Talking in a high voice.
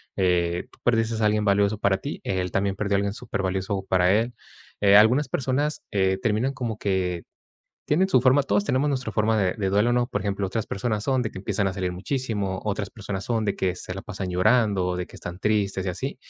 No: low, 100 Hz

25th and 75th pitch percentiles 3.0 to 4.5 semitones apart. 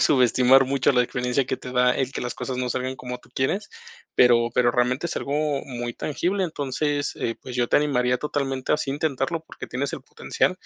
No: narrow, 2.5 semitones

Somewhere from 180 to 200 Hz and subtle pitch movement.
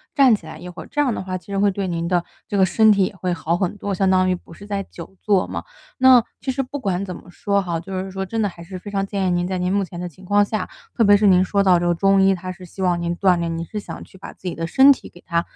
Yes: high, 190 Hz; narrow, 2.3 semitones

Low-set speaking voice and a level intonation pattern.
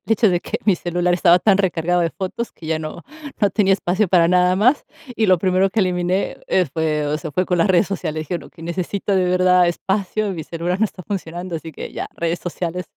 No: medium, 180 Hz; narrow, 2.2 semitones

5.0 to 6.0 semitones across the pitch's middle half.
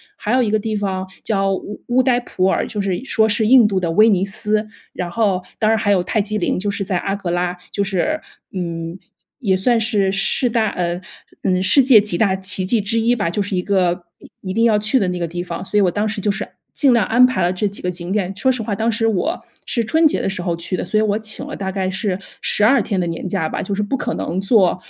No: average, 3.1 semitones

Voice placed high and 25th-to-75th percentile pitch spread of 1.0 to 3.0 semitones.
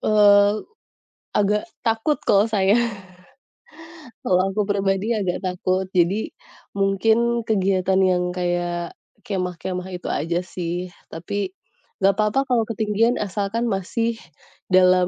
Yes: high, 195 Hz; average, 2.7 semitones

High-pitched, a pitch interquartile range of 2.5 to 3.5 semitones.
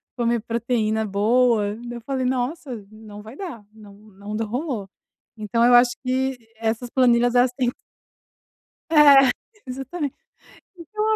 Yes: high, 240 Hz; average, 3.1 semitones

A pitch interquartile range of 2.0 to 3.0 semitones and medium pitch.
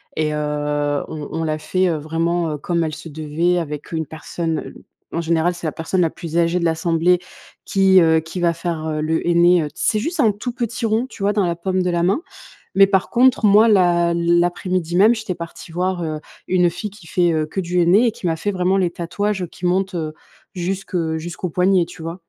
Yes: average, 2.7 semitones; medium, 175 Hz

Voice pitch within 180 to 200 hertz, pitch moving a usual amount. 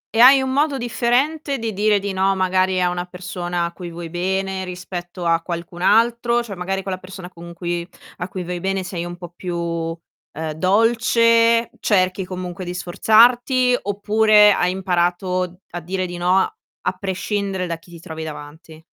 Yes: medium, 185 Hz; average, 3.5 semitones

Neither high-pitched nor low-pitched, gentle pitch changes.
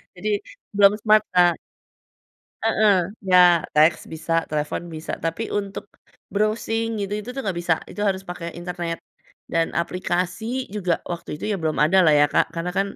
No: medium, 180 Hz; average, 3.7 semitones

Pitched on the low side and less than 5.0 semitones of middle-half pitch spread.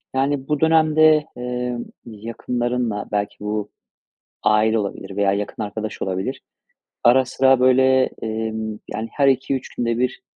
Yes: low, 120 Hz; average, 3.6 semitones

